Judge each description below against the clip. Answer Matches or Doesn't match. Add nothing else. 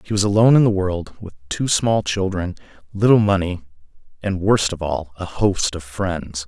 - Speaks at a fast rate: Doesn't match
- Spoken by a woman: Doesn't match